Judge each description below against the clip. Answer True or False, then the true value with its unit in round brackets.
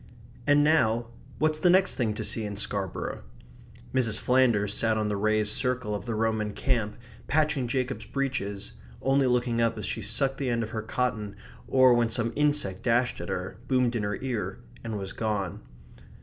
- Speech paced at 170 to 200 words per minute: True (180 wpm)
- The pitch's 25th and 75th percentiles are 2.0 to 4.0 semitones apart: True (3.5 semitones)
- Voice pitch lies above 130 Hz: False (115 Hz)